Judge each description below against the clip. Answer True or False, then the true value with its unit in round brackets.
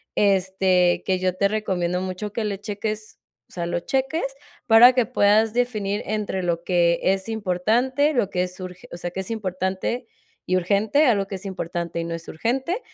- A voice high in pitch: True (195 Hz)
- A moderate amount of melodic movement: True (3.6 semitones)